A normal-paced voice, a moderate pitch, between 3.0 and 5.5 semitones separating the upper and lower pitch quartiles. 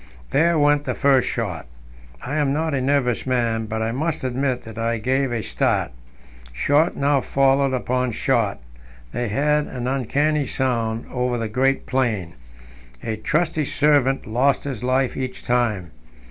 No: average, 155 wpm; low, 130 Hz; average, 3.3 semitones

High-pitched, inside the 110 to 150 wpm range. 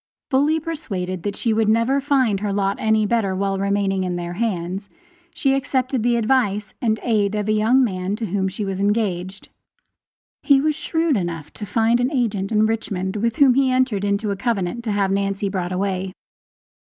No: high, 210 Hz; average, 190 wpm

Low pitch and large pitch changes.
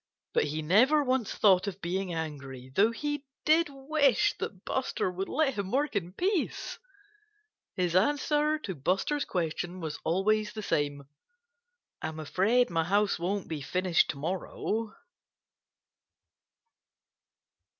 No: high, 195 Hz; wide, 7.7 semitones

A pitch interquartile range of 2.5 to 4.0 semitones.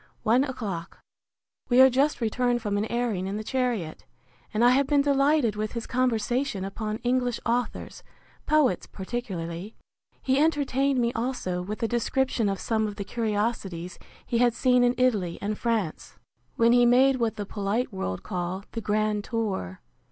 Yes: average, 3.6 semitones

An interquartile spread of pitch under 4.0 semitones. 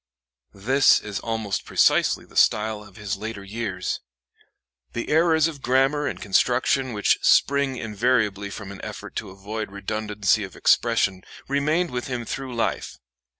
No: average, 4.6 semitones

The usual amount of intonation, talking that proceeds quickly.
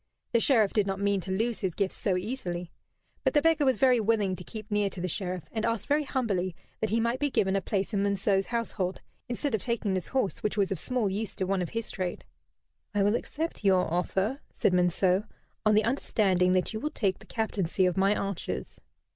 Yes: average, 3.5 semitones; fast, 220 wpm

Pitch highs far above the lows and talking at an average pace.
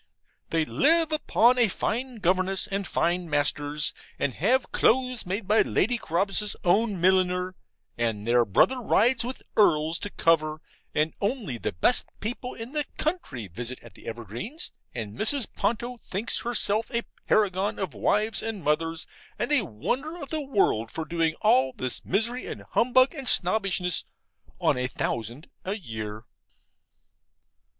Yes: wide, 7.8 semitones; average, 150 wpm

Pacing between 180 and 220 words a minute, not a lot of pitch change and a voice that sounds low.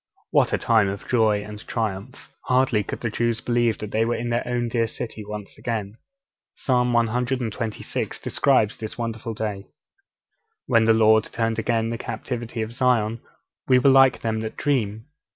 No: average, 170 wpm; narrow, 1.7 semitones; low, 115 Hz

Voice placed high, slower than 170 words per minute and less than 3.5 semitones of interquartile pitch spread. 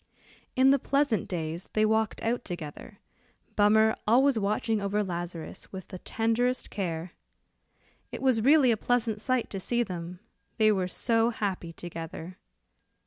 No: high, 215 Hz; average, 140 wpm; average, 4.7 semitones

